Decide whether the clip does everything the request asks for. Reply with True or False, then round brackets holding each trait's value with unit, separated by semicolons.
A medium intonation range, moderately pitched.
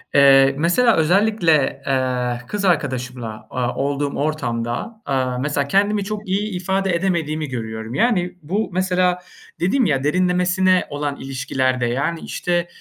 False (5.9 semitones; 155 Hz)